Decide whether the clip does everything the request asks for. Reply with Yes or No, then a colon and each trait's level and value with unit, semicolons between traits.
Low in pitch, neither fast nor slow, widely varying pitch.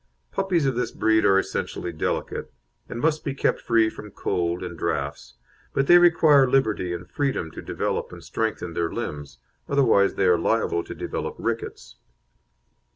Yes: low, 110 Hz; average, 160 wpm; wide, 7.9 semitones